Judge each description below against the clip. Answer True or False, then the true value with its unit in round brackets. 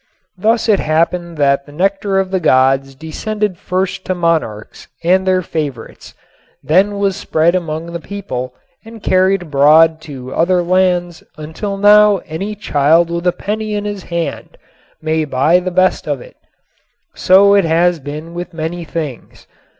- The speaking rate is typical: True (160 wpm)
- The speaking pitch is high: False (175 Hz)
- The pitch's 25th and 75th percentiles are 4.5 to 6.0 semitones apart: False (3.6 semitones)